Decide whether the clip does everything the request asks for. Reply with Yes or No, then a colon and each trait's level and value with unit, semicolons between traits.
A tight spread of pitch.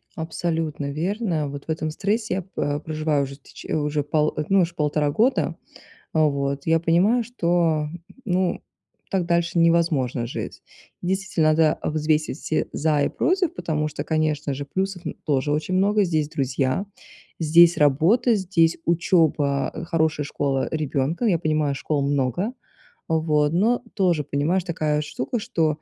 No: average, 3.1 semitones